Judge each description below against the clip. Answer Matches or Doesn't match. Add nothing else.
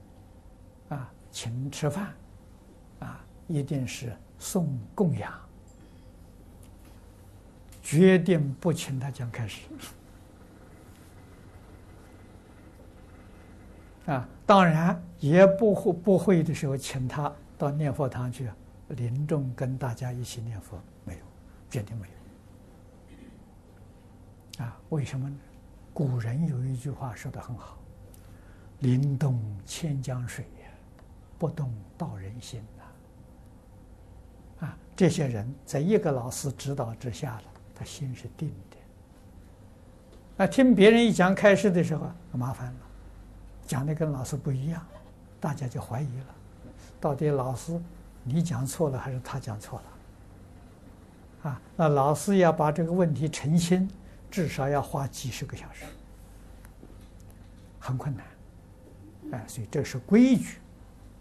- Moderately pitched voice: Doesn't match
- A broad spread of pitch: Matches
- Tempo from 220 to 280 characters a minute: Doesn't match